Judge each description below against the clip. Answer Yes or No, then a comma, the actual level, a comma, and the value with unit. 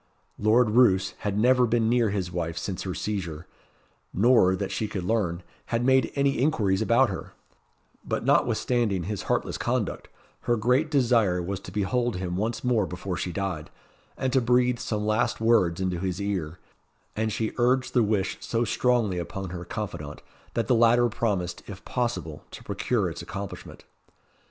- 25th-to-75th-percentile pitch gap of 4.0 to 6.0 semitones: Yes, average, 4.5 semitones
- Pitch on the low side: Yes, low, 105 Hz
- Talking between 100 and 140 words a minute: No, average, 165 wpm